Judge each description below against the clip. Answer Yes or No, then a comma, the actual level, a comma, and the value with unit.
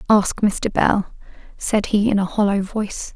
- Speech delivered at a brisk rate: No, average, 170 wpm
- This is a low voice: No, high, 205 Hz